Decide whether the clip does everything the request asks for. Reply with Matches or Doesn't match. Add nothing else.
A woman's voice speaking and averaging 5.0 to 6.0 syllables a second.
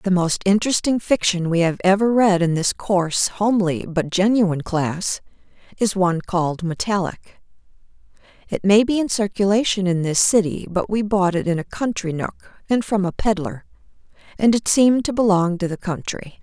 Matches